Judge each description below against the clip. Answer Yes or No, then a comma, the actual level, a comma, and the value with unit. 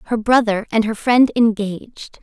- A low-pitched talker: No, high, 220 Hz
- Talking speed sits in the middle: Yes, average, 160 wpm